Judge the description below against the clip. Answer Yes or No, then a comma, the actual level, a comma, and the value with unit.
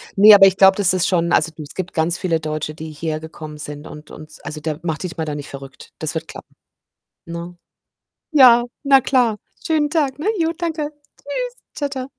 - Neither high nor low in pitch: Yes, medium, 175 Hz